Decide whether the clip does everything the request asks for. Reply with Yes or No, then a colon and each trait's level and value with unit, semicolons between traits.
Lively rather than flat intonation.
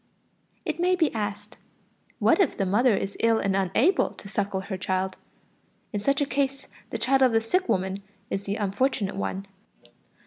Yes: wide, 5.7 semitones